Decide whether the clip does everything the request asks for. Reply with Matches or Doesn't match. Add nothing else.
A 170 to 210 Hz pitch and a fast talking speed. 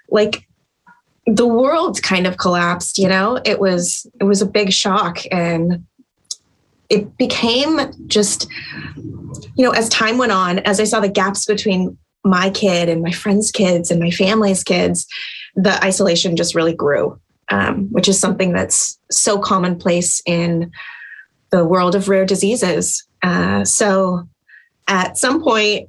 Doesn't match